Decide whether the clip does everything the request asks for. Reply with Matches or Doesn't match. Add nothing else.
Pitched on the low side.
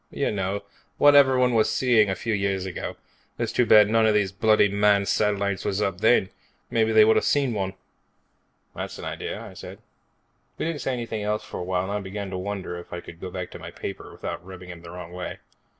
Matches